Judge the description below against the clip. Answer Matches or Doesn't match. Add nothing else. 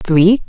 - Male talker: Doesn't match